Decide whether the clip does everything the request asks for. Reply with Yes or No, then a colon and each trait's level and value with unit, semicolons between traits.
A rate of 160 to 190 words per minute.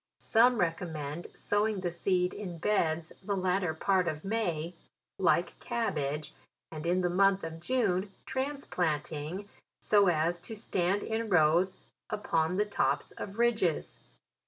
No: slow, 135 wpm